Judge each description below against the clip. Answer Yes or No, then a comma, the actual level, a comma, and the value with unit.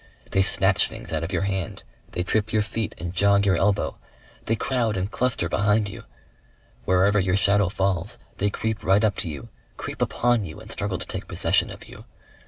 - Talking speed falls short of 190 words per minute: No, average, 195 wpm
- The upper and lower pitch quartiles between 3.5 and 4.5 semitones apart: No, narrow, 2.4 semitones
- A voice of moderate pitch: No, low, 100 Hz